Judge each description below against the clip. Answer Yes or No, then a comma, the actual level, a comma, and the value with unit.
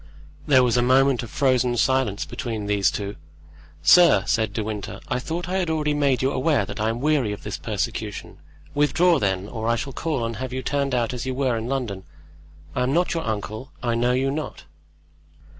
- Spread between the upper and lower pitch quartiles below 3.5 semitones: No, average, 3.9 semitones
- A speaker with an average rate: No, fast, 210 wpm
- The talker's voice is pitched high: No, low, 125 Hz